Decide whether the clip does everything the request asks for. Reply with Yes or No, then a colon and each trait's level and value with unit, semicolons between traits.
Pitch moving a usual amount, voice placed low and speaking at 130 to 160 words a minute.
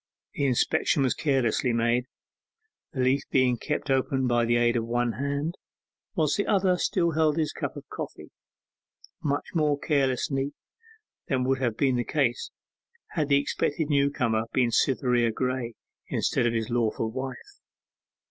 Yes: average, 3.2 semitones; low, 130 Hz; average, 155 wpm